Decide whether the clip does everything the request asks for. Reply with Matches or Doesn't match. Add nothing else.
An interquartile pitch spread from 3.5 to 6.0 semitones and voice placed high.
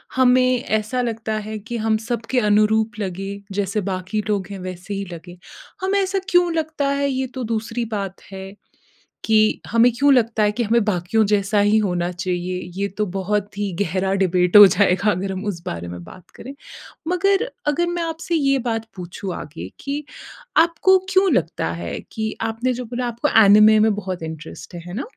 Matches